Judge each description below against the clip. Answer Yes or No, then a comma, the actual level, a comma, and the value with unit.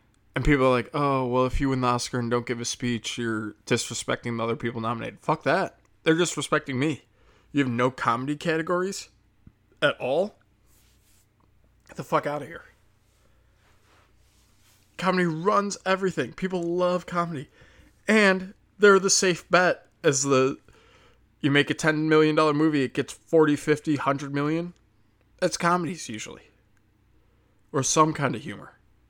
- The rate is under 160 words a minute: Yes, average, 150 wpm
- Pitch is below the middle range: Yes, low, 130 Hz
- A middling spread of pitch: No, wide, 6.6 semitones